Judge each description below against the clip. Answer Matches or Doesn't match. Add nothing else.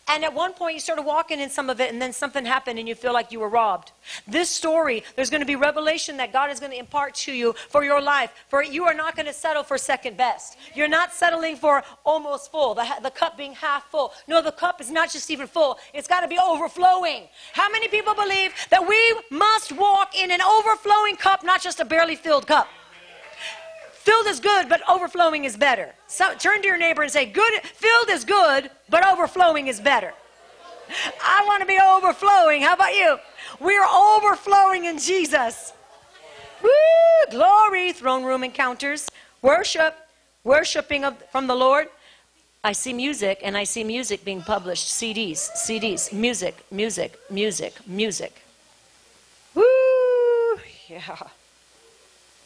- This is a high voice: Matches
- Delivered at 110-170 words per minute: Doesn't match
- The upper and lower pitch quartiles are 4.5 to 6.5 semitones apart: Matches